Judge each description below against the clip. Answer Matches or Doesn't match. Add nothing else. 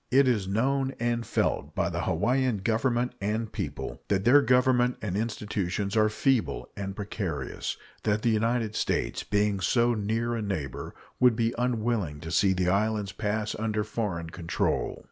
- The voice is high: Doesn't match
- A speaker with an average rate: Matches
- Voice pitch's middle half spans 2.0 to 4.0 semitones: Matches